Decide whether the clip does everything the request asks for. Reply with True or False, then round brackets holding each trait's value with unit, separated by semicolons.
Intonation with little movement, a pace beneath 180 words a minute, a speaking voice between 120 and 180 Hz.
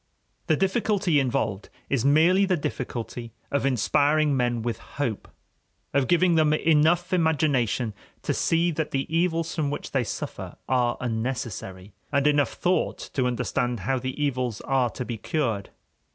False (4.8 semitones; 150 wpm; 140 Hz)